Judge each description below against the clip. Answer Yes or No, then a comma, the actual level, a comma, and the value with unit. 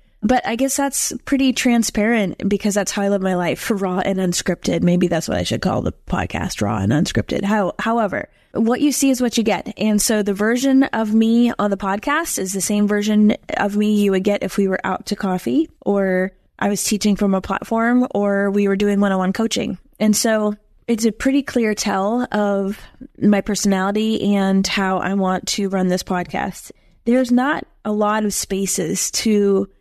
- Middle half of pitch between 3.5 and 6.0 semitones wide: No, average, 2.8 semitones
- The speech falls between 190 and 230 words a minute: Yes, average, 200 wpm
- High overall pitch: Yes, high, 205 Hz